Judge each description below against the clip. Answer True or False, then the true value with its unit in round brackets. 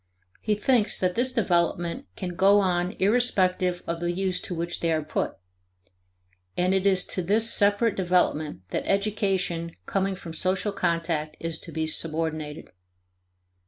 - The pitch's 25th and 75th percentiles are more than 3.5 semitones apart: False (2.9 semitones)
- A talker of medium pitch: True (180 Hz)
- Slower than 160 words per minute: True (150 wpm)